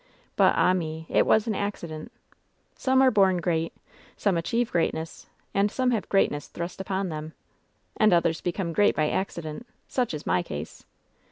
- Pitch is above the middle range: No, medium, 180 Hz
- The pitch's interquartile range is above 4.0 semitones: Yes, average, 4.4 semitones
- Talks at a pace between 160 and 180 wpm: Yes, average, 170 wpm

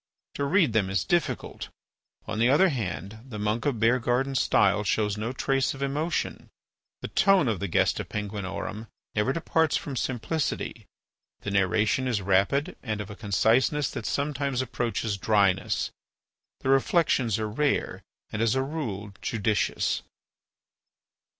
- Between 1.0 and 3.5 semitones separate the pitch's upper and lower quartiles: No, average, 4.8 semitones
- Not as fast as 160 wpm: Yes, average, 140 wpm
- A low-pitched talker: Yes, low, 115 Hz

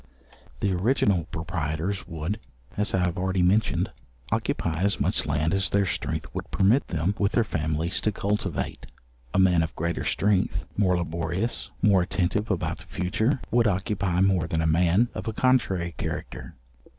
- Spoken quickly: No, average, 165 wpm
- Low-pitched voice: Yes, very low, 95 Hz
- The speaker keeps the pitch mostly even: No, average, 3.2 semitones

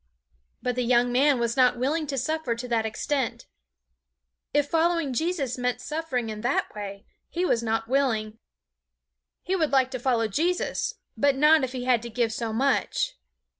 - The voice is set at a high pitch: Yes, very high, 255 Hz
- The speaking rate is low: No, average, 170 wpm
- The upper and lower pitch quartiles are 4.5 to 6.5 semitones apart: No, average, 3.9 semitones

